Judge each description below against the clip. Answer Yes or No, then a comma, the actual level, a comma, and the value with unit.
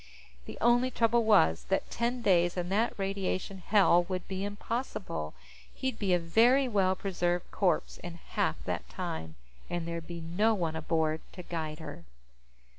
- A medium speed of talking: Yes, average, 160 wpm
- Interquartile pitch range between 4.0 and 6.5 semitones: Yes, average, 4.3 semitones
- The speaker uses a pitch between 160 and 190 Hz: Yes, medium, 185 Hz